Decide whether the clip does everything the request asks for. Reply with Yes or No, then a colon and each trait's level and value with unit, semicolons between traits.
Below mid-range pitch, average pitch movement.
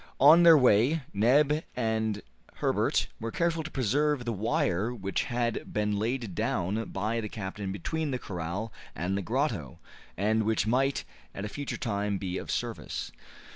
Yes: low, 110 Hz; average, 4.9 semitones